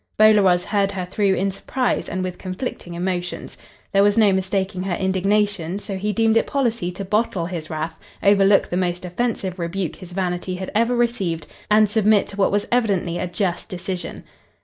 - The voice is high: Yes, high, 195 Hz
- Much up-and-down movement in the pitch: No, average, 2.7 semitones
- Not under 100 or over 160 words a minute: No, average, 180 wpm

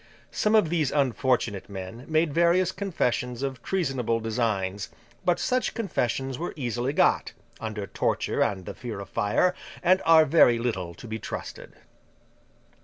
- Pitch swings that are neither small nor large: No, wide, 7.0 semitones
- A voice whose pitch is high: No, low, 125 Hz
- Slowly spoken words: No, average, 145 wpm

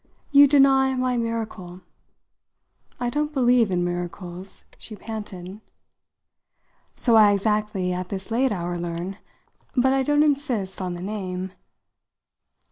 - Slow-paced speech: Yes, slow, 125 wpm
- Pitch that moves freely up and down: Yes, wide, 5.7 semitones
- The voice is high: Yes, high, 210 Hz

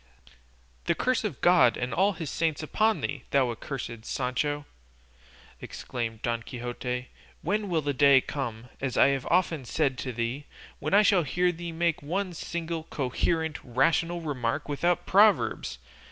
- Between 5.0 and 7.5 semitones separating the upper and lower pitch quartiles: Yes, average, 5.3 semitones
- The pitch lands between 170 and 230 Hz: No, medium, 145 Hz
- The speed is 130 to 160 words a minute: Yes, average, 155 wpm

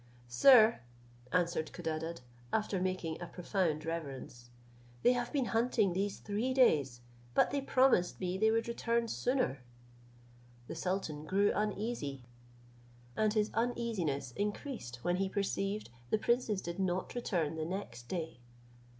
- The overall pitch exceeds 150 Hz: Yes, high, 190 Hz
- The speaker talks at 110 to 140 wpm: Yes, slow, 135 wpm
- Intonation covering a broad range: Yes, wide, 5.8 semitones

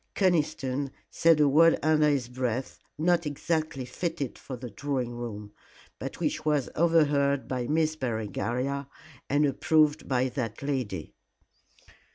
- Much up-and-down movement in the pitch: No, average, 3.7 semitones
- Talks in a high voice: No, medium, 140 Hz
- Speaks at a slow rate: Yes, slow, 130 wpm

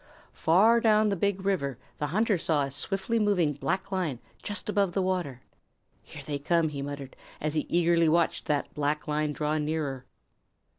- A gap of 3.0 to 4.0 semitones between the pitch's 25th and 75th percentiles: No, average, 4.8 semitones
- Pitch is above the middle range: No, medium, 160 Hz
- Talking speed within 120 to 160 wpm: No, average, 170 wpm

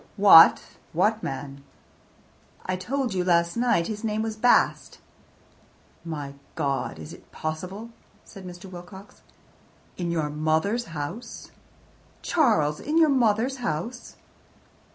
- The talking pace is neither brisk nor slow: No, slow, 115 wpm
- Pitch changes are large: Yes, wide, 6.2 semitones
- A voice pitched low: No, medium, 185 Hz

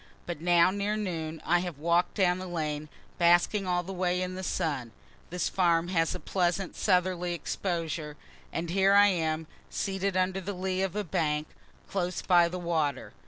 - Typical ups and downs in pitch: No, narrow, 2.2 semitones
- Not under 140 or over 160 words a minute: No, average, 175 wpm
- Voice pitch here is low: No, medium, 175 Hz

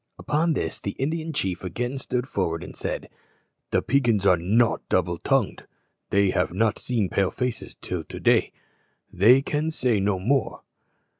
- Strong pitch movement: Yes, wide, 6.1 semitones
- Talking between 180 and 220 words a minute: No, average, 160 wpm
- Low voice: Yes, low, 115 Hz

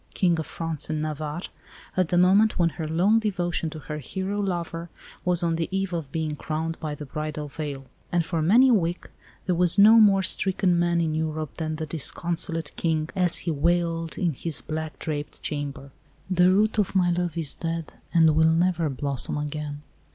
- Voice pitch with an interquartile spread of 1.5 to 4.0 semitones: Yes, narrow, 2.6 semitones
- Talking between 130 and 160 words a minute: No, average, 190 wpm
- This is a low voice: No, medium, 165 Hz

